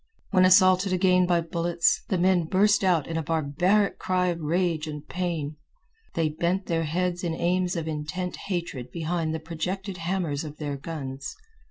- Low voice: No, medium, 170 Hz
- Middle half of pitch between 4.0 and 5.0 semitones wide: No, narrow, 2.6 semitones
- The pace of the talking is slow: No, average, 170 wpm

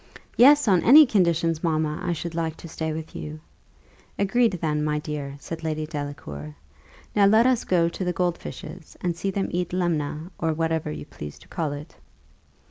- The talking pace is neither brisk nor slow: Yes, average, 185 wpm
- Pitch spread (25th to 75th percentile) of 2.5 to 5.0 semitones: Yes, average, 3.1 semitones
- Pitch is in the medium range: Yes, medium, 165 Hz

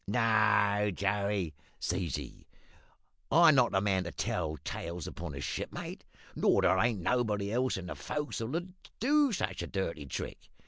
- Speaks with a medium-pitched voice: No, low, 100 Hz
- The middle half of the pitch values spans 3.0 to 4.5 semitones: No, wide, 5.5 semitones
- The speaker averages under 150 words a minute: No, average, 155 wpm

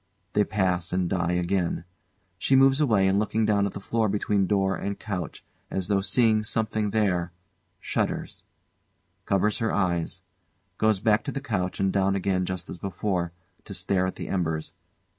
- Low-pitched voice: Yes, low, 100 Hz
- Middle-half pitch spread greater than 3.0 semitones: No, average, 2.7 semitones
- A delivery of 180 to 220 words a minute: No, average, 170 wpm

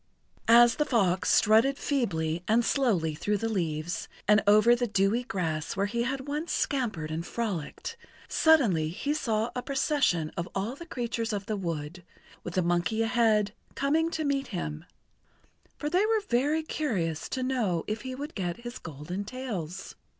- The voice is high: Yes, high, 220 Hz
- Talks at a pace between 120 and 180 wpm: Yes, average, 165 wpm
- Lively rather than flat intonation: Yes, wide, 6.8 semitones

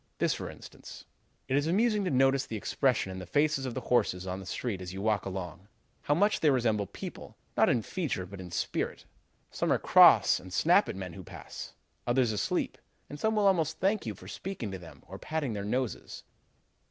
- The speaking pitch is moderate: No, low, 115 Hz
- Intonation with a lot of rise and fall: Yes, wide, 7.6 semitones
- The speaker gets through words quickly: Yes, fast, 215 wpm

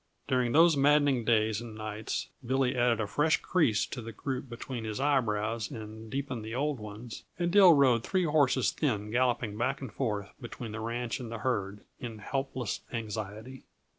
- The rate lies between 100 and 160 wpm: No, average, 175 wpm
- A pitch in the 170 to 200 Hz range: No, low, 120 Hz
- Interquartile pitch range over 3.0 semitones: Yes, average, 3.7 semitones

